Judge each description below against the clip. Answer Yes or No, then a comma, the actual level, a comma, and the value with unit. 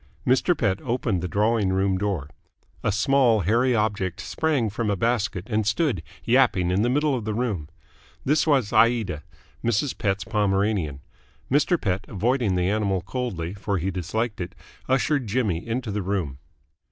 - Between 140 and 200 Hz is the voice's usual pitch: No, low, 105 Hz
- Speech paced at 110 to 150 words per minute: No, average, 160 wpm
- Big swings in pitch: No, average, 4.3 semitones